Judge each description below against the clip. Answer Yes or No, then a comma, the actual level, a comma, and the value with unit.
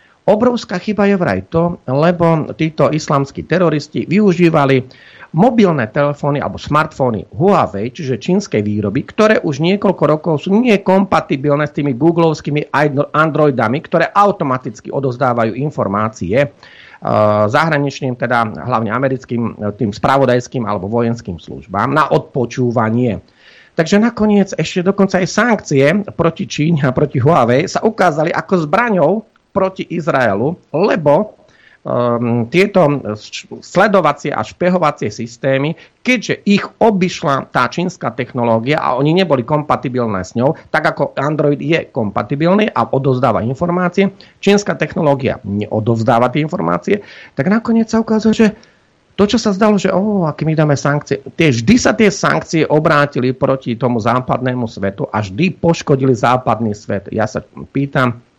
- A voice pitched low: No, medium, 150 Hz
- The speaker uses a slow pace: No, average, 130 wpm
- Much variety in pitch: Yes, wide, 6.3 semitones